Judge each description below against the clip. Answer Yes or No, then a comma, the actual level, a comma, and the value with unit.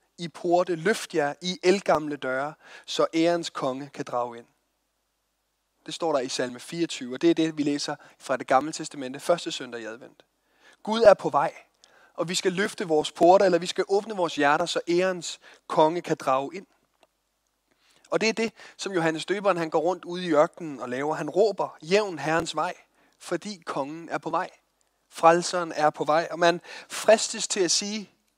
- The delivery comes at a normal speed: Yes, average, 190 wpm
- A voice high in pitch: No, medium, 165 Hz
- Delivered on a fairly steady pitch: No, average, 3.4 semitones